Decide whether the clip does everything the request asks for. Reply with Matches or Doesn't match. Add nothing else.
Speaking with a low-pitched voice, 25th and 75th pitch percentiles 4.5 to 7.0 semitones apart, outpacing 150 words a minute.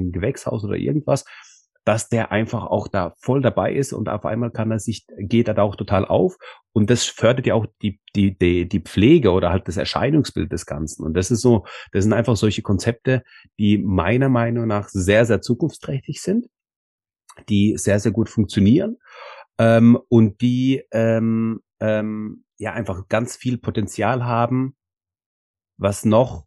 Doesn't match